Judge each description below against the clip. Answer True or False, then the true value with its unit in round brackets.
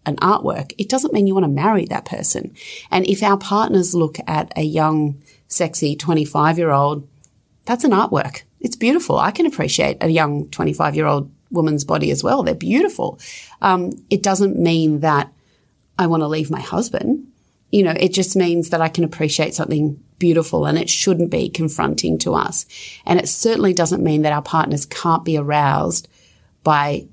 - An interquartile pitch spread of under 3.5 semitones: False (4.3 semitones)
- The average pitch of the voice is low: False (160 Hz)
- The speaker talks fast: False (185 wpm)